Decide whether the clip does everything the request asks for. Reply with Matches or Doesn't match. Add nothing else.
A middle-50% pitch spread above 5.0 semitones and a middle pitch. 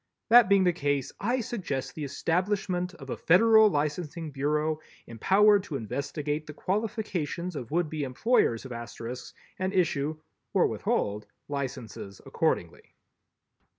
Matches